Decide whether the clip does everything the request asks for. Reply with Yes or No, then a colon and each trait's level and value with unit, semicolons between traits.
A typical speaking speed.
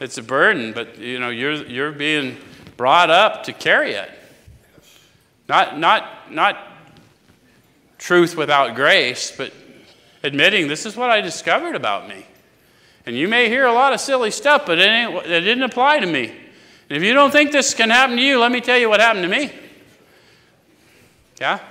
Yes: average, 180 wpm